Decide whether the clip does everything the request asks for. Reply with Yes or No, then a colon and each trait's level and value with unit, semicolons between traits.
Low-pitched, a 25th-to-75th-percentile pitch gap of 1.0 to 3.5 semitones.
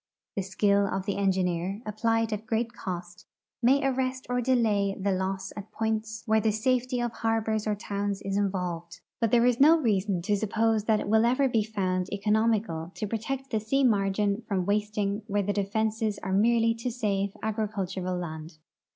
No: high, 210 Hz; narrow, 2.6 semitones